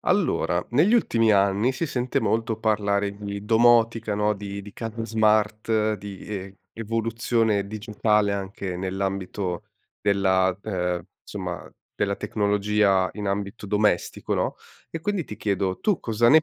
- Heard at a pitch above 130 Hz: No, low, 105 Hz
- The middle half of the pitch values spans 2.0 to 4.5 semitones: Yes, narrow, 2.4 semitones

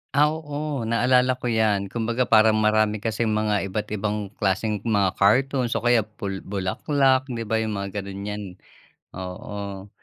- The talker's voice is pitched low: Yes, low, 110 Hz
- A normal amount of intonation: Yes, average, 3.2 semitones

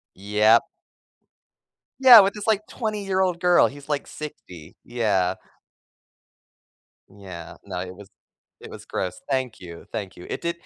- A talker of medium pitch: No, low, 120 Hz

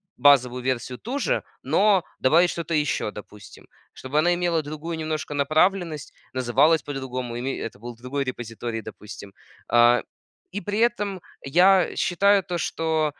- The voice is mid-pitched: Yes, medium, 150 Hz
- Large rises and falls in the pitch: Yes, wide, 5.9 semitones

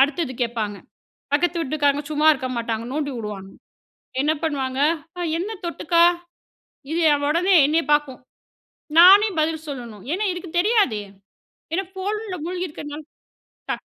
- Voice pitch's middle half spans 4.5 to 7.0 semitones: Yes, average, 5.0 semitones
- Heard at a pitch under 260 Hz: No, very high, 305 Hz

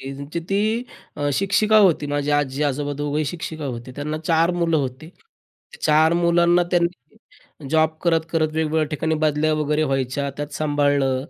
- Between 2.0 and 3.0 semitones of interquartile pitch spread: Yes, average, 2.7 semitones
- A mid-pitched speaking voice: Yes, medium, 155 Hz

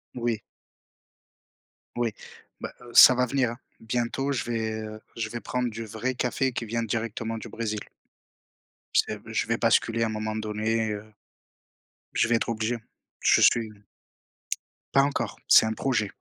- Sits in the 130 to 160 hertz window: No, low, 115 Hz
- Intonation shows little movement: Yes, narrow, 1.7 semitones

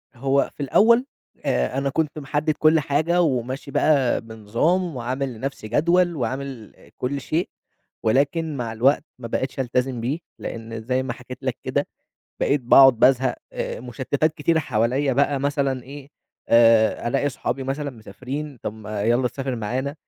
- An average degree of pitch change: Yes, average, 3.2 semitones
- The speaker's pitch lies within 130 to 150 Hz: Yes, low, 135 Hz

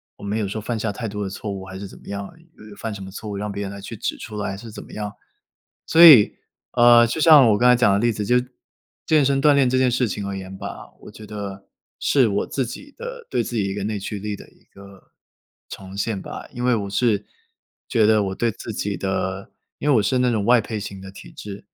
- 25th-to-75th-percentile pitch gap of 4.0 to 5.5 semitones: No, average, 3.3 semitones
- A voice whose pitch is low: Yes, low, 105 Hz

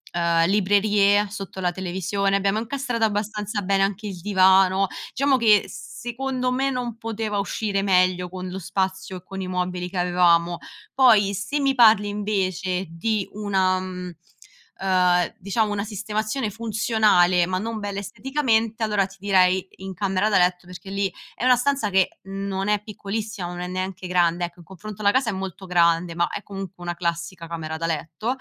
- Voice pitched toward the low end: No, high, 195 Hz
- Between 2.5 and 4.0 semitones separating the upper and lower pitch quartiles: Yes, average, 2.8 semitones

